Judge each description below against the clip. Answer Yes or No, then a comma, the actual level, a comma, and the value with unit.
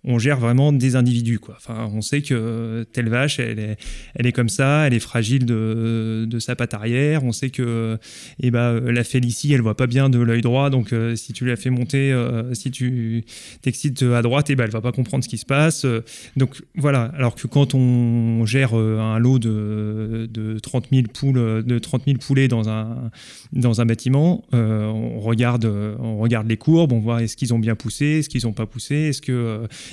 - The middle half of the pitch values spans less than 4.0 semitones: Yes, narrow, 2.5 semitones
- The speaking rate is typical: No, fast, 225 wpm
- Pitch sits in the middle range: No, low, 120 Hz